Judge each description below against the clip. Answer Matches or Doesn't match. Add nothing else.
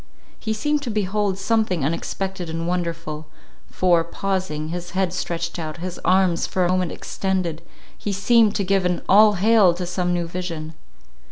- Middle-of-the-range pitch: Matches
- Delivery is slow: Doesn't match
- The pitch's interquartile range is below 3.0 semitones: Matches